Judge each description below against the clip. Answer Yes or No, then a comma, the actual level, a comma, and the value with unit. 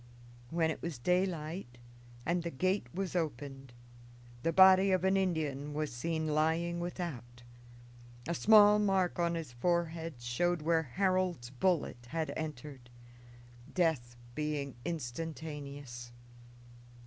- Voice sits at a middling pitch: Yes, medium, 160 Hz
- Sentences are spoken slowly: Yes, slow, 115 wpm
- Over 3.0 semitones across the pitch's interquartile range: Yes, average, 4.0 semitones